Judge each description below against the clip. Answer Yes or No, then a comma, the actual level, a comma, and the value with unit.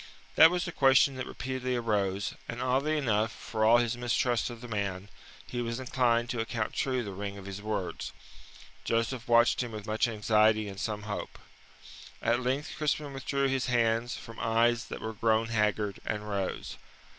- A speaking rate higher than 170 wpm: Yes, average, 180 wpm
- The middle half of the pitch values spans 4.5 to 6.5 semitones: No, average, 2.9 semitones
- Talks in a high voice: No, low, 115 Hz